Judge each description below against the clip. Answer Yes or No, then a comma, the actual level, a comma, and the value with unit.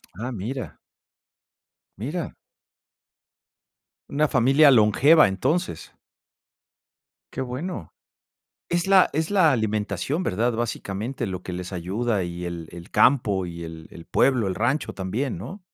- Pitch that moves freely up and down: Yes, wide, 7.1 semitones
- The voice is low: Yes, low, 115 Hz